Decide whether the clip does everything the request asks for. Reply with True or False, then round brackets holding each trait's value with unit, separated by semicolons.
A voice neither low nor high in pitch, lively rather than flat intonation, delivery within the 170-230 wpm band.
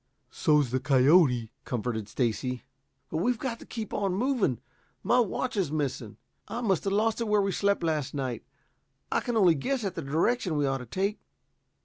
True (165 Hz; 8.1 semitones; 190 wpm)